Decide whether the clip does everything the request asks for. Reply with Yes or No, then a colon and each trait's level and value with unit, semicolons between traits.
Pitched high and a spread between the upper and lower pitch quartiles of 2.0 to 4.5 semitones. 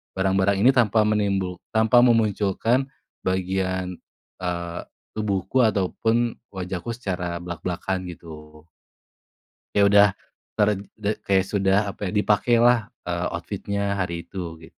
No: very low, 95 Hz; average, 2.9 semitones